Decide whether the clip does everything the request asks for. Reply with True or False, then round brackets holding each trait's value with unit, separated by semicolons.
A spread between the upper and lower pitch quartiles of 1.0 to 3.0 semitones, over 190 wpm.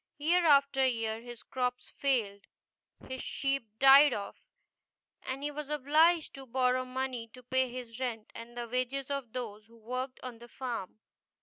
False (2.7 semitones; 165 wpm)